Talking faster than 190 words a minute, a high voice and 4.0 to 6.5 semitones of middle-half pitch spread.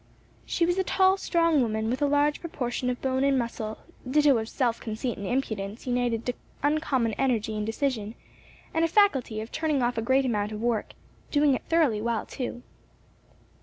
No: average, 185 wpm; very high, 250 Hz; average, 4.5 semitones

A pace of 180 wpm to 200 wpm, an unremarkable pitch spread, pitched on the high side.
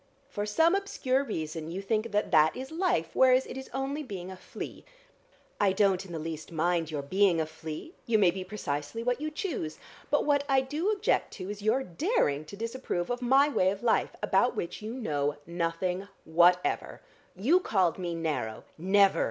No: average, 195 wpm; wide, 7.8 semitones; high, 200 Hz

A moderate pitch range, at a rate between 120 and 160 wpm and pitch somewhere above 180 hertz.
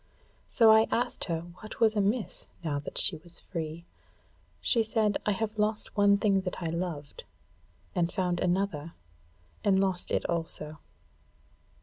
Yes: average, 4.1 semitones; average, 145 wpm; high, 190 Hz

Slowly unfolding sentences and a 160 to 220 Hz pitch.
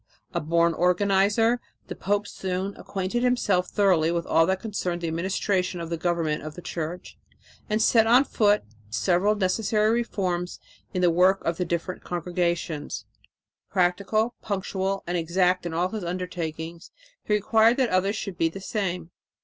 No: average, 155 wpm; medium, 185 Hz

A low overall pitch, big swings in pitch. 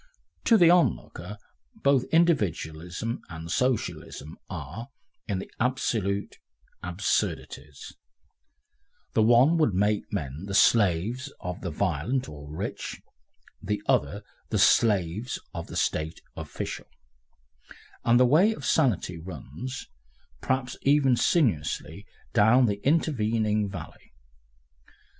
Yes: low, 105 Hz; wide, 6.6 semitones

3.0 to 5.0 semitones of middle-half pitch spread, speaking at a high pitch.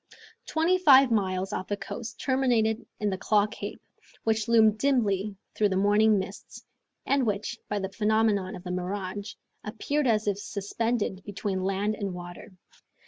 No: narrow, 2.6 semitones; high, 210 Hz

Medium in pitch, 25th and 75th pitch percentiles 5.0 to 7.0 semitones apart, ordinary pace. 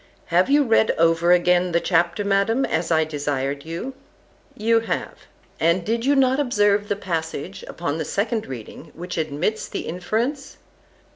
Yes: medium, 180 Hz; wide, 5.5 semitones; average, 150 wpm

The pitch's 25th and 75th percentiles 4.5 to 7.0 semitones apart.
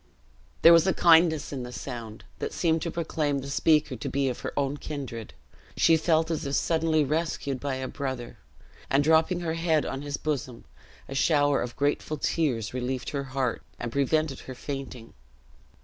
No: average, 3.4 semitones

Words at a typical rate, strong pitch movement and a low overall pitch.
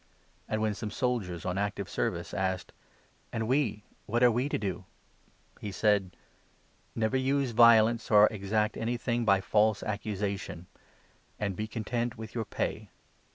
No: average, 160 wpm; average, 2.7 semitones; low, 110 Hz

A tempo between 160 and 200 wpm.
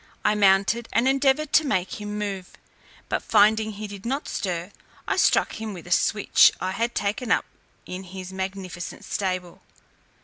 Yes: average, 165 wpm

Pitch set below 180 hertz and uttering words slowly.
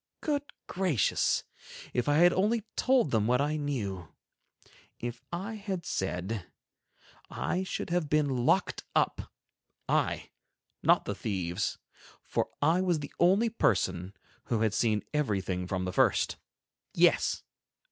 Yes: medium, 140 Hz; slow, 115 wpm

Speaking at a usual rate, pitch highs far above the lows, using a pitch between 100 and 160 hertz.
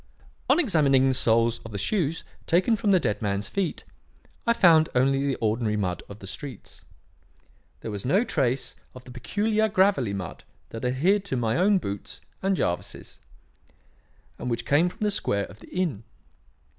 Yes: average, 170 wpm; wide, 8.9 semitones; low, 135 Hz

